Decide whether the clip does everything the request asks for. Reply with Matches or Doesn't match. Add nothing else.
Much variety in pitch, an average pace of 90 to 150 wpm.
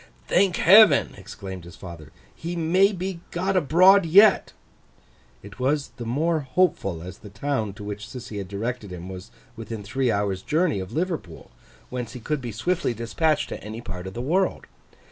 Doesn't match